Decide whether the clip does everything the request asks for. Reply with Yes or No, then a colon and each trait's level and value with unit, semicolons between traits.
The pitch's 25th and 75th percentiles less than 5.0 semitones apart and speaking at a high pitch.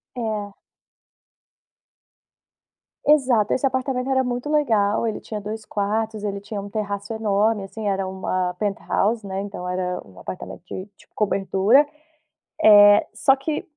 Yes: average, 2.8 semitones; high, 210 Hz